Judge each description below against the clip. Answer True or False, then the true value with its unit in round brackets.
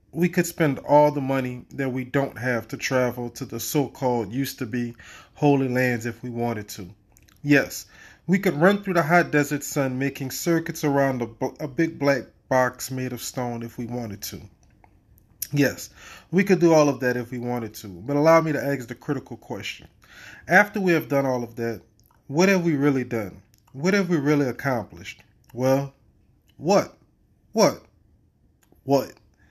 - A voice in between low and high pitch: False (130 Hz)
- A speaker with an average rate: True (180 wpm)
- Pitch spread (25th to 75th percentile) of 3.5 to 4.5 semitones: True (3.8 semitones)